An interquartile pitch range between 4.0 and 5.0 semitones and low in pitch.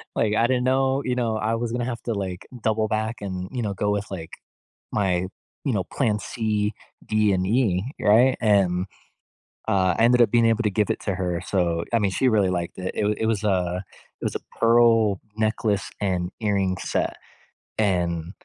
No: average, 3.6 semitones; low, 105 Hz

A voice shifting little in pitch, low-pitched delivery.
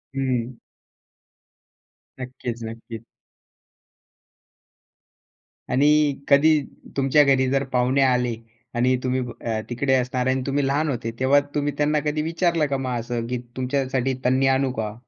Yes: narrow, 2.1 semitones; low, 130 Hz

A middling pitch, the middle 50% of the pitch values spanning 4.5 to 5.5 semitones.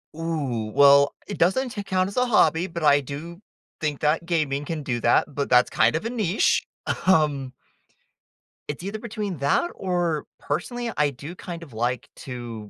Yes: medium, 160 Hz; average, 4.9 semitones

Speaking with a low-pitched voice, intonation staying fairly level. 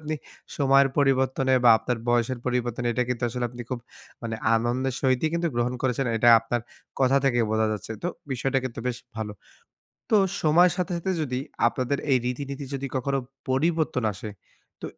Yes: low, 130 Hz; narrow, 2.3 semitones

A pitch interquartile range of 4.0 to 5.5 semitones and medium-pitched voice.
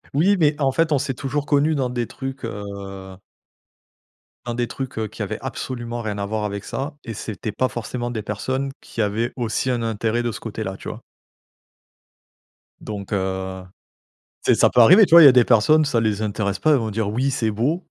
No: average, 4.4 semitones; low, 120 Hz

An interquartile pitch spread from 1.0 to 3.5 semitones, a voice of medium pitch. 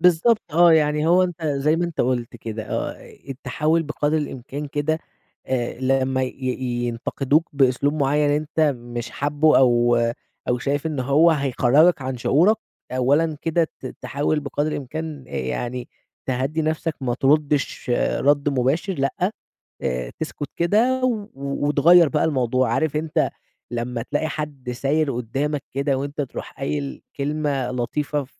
Yes: average, 3.2 semitones; medium, 145 Hz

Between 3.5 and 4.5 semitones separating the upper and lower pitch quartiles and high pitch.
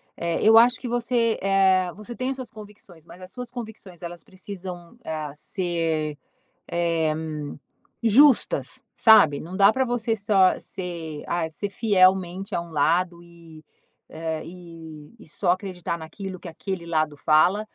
No: average, 4.0 semitones; medium, 180 Hz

